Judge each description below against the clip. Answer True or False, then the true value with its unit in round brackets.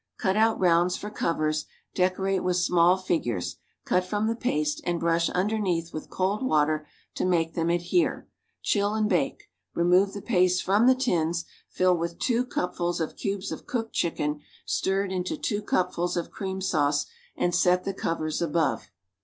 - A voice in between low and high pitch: True (180 Hz)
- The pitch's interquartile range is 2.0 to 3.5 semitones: True (2.9 semitones)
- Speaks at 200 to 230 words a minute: False (165 wpm)